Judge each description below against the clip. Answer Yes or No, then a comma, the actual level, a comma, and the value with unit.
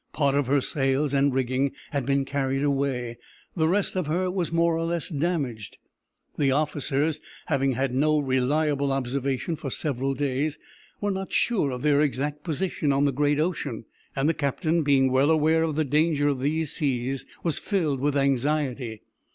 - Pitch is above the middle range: No, medium, 145 Hz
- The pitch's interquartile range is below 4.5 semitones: Yes, narrow, 2.6 semitones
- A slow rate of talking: No, average, 175 wpm